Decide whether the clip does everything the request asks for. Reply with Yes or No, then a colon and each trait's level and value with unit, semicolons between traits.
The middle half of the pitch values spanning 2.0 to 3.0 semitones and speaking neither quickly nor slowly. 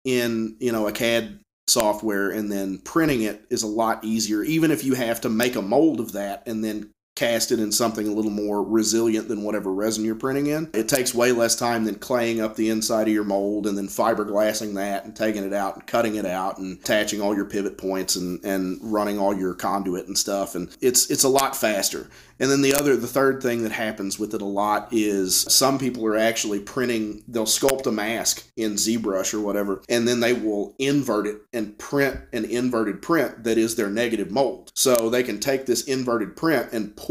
No: narrow, 2.5 semitones; fast, 220 wpm